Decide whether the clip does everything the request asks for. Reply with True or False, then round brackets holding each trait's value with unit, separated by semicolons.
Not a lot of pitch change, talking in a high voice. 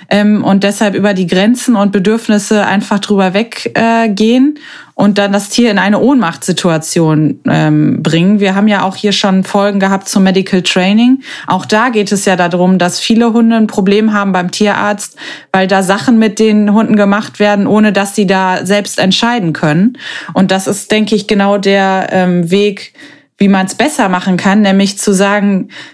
True (2.0 semitones; 200 Hz)